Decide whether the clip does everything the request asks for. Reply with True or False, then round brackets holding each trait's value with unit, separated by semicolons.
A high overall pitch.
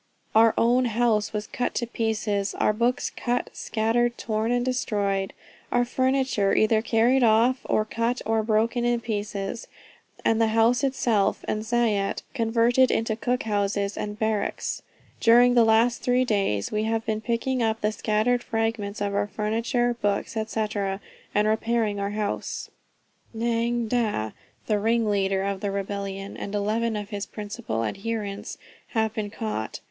True (220 Hz)